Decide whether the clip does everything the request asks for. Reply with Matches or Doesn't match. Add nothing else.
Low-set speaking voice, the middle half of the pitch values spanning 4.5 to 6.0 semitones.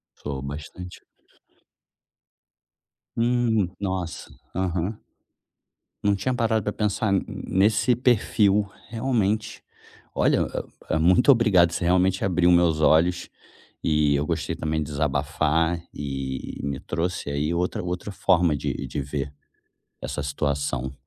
Matches